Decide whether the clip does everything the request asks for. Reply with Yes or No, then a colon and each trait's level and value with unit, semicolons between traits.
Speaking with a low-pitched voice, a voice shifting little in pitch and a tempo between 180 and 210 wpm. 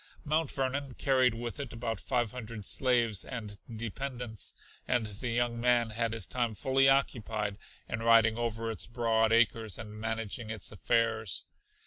No: low, 115 Hz; narrow, 1.9 semitones; average, 150 wpm